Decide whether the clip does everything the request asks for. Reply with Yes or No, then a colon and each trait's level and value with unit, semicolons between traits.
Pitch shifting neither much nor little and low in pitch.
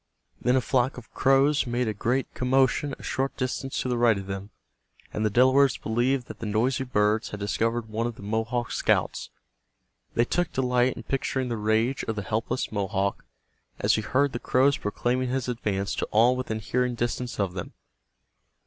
Yes: average, 3.0 semitones; low, 120 Hz